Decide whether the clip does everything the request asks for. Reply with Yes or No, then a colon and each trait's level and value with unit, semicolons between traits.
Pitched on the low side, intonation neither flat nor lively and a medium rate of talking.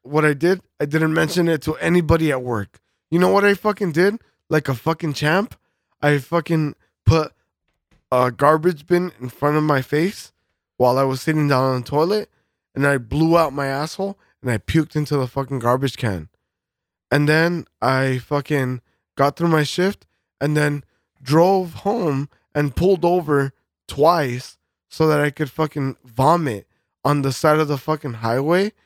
No: medium, 150 Hz; average, 3.6 semitones; average, 175 wpm